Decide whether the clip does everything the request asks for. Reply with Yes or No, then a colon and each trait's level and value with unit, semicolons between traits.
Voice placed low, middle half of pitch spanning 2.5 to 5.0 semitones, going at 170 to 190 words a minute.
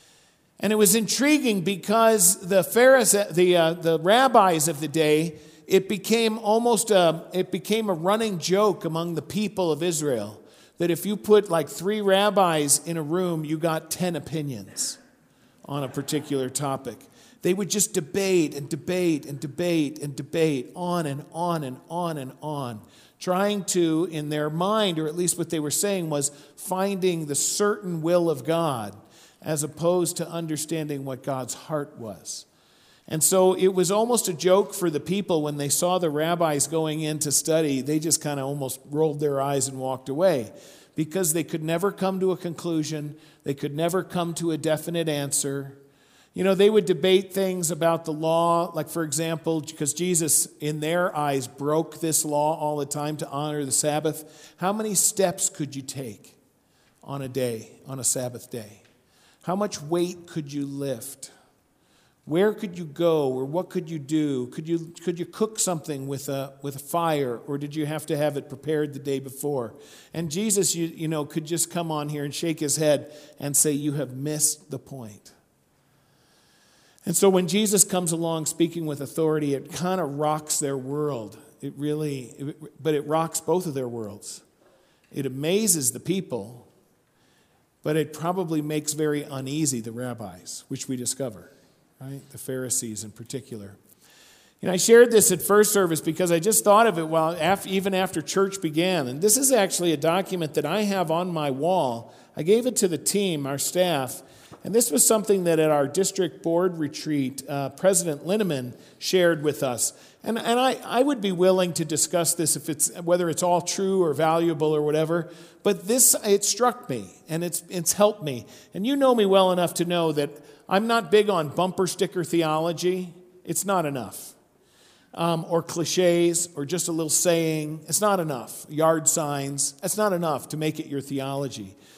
No: medium, 160 Hz; average, 4.0 semitones; average, 185 wpm